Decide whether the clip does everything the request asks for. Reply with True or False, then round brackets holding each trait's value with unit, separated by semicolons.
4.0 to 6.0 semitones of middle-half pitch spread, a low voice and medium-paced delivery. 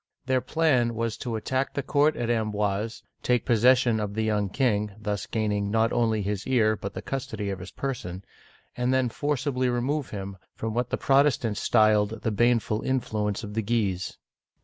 False (3.4 semitones; 115 Hz; 185 wpm)